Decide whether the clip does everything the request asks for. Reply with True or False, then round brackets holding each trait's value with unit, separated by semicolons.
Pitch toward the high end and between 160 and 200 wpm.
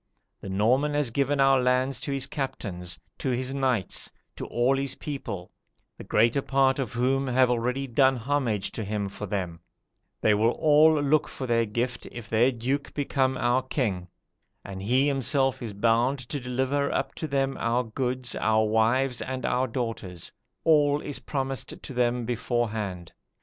False (125 Hz; 165 wpm)